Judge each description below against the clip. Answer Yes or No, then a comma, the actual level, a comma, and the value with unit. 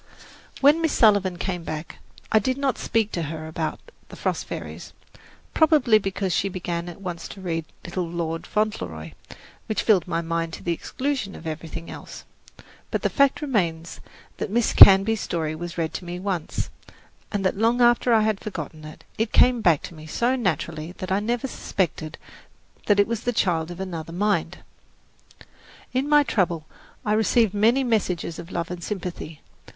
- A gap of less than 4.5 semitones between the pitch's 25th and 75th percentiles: No, average, 4.9 semitones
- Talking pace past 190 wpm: No, average, 175 wpm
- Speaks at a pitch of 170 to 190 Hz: Yes, medium, 185 Hz